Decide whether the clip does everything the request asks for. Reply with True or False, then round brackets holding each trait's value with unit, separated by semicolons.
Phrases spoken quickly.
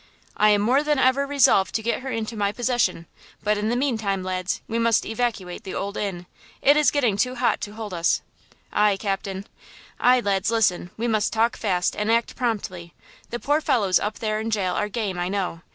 True (210 wpm)